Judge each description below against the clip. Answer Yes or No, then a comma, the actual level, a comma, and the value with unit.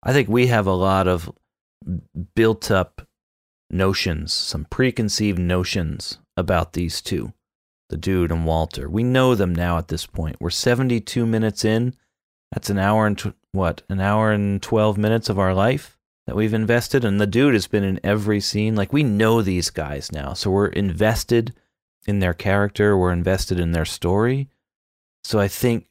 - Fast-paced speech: No, average, 175 wpm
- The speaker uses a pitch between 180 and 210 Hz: No, low, 100 Hz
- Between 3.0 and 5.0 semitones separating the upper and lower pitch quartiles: Yes, average, 3.7 semitones